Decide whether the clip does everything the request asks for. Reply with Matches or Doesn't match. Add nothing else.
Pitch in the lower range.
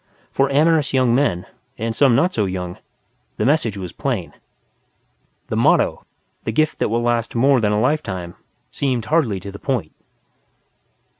Matches